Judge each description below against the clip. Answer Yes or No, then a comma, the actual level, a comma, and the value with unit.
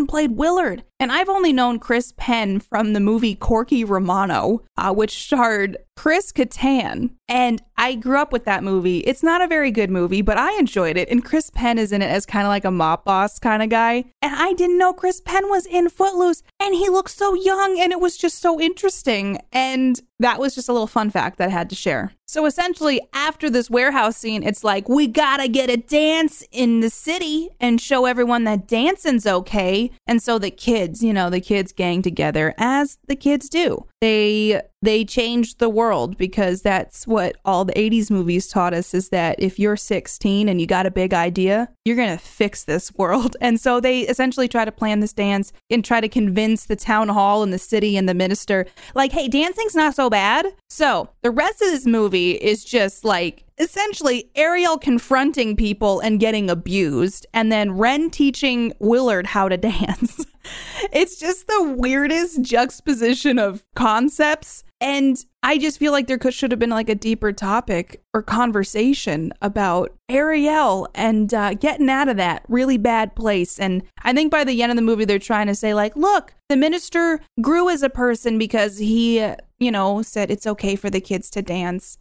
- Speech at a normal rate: Yes, average, 195 wpm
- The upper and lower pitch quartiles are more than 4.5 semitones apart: Yes, wide, 5.6 semitones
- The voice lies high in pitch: Yes, high, 230 Hz